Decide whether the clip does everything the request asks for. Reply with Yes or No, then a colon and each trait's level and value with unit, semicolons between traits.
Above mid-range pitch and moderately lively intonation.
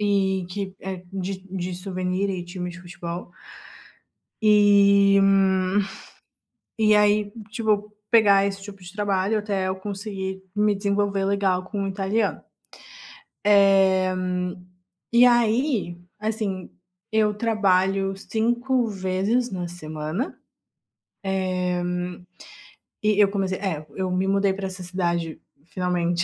No: high, 195 Hz; narrow, 2.0 semitones